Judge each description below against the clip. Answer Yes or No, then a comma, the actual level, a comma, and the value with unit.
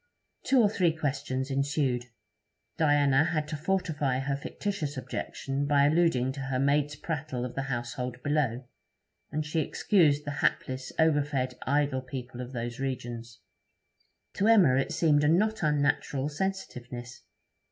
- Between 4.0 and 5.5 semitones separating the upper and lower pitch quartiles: No, average, 3.0 semitones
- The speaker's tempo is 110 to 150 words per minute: Yes, average, 140 wpm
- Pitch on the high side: No, medium, 140 Hz